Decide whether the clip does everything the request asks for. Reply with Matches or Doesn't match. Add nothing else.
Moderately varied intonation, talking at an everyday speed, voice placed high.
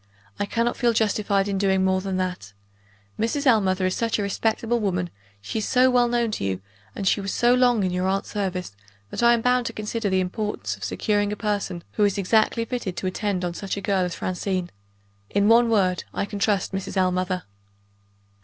Doesn't match